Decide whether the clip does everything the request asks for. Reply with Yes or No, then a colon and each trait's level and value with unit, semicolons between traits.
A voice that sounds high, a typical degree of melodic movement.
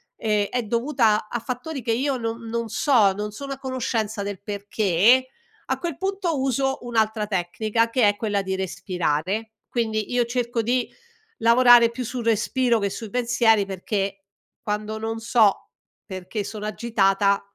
Yes: high, 225 Hz; average, 3.0 semitones